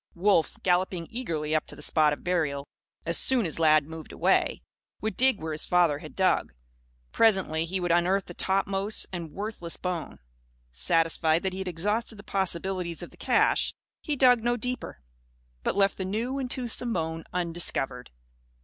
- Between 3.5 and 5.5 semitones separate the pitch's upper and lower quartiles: Yes, average, 4.2 semitones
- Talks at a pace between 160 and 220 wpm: Yes, average, 170 wpm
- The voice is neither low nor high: Yes, medium, 180 Hz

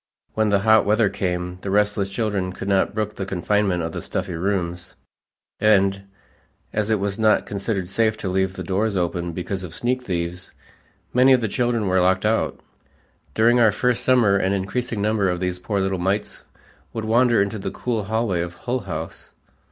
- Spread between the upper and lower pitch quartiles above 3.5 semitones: No, average, 2.9 semitones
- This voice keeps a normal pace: Yes, average, 185 wpm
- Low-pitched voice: Yes, low, 100 Hz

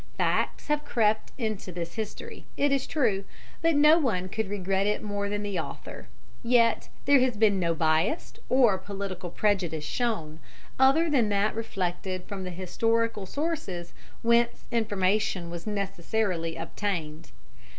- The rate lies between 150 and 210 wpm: No, average, 140 wpm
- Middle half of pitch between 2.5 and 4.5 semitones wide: Yes, average, 4.2 semitones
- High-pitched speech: Yes, high, 205 Hz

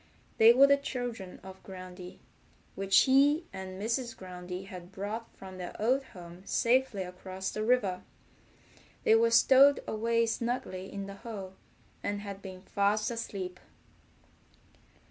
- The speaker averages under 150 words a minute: Yes, slow, 135 wpm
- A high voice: Yes, high, 200 Hz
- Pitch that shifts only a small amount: No, average, 3.8 semitones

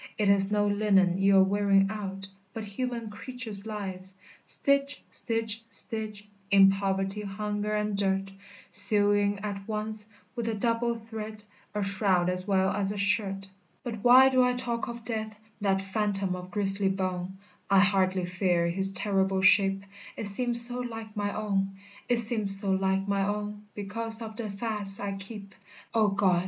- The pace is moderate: Yes, average, 160 wpm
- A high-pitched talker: Yes, high, 205 Hz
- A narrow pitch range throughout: Yes, narrow, 2.0 semitones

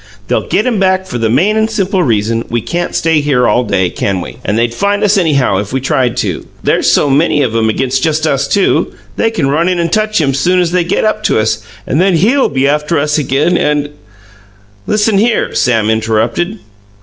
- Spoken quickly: Yes, fast, 220 wpm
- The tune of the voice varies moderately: No, wide, 7.8 semitones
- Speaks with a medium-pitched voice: Yes, medium, 150 Hz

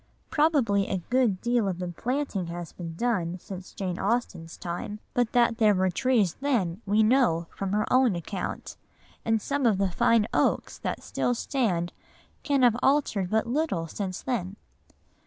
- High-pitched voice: Yes, high, 210 Hz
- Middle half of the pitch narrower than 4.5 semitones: No, average, 5.2 semitones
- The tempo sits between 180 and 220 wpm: No, average, 165 wpm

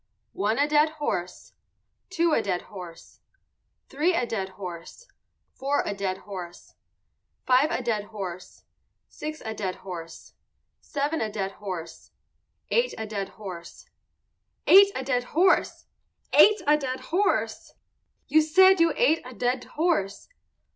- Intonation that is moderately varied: No, wide, 8.2 semitones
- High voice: Yes, high, 245 Hz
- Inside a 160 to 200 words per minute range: No, slow, 135 wpm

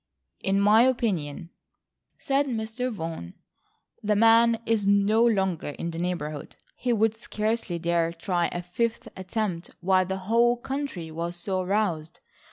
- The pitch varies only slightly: No, average, 4.7 semitones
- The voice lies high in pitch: Yes, high, 200 Hz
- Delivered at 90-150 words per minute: Yes, average, 140 wpm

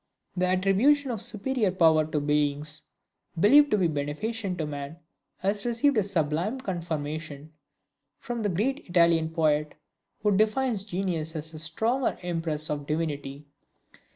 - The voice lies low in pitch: No, medium, 175 Hz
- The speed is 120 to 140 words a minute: Yes, slow, 135 wpm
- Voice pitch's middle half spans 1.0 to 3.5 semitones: No, wide, 5.6 semitones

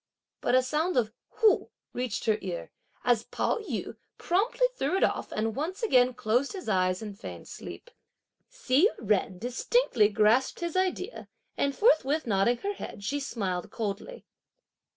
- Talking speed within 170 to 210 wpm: No, average, 150 wpm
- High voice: Yes, very high, 255 Hz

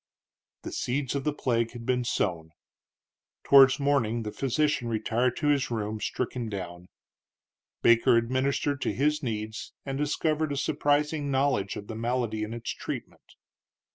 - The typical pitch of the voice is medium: No, low, 125 Hz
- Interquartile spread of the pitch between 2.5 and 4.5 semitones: Yes, average, 4.1 semitones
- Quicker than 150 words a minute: No, average, 145 wpm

